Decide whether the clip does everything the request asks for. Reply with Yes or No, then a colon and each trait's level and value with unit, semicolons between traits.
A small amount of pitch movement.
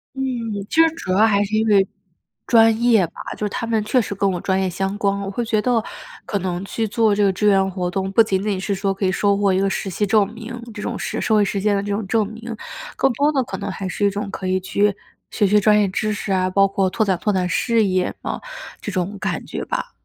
Yes: narrow, 2.2 semitones